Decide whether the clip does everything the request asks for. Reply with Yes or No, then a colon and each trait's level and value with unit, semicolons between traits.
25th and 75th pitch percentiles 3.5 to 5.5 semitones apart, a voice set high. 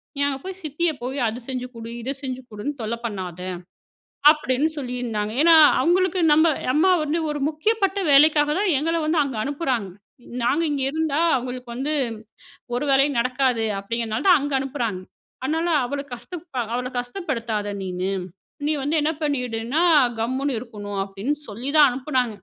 Yes: average, 4.6 semitones; very high, 265 Hz